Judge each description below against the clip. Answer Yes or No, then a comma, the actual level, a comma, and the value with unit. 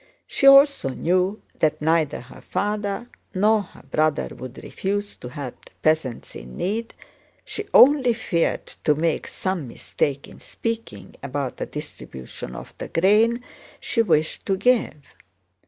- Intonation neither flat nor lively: No, wide, 7.4 semitones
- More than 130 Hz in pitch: Yes, medium, 185 Hz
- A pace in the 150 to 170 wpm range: No, average, 140 wpm